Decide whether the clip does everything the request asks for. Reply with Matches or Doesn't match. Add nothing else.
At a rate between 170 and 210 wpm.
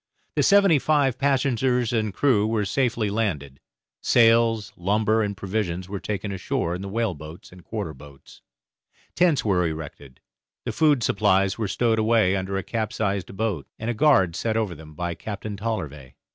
Doesn't match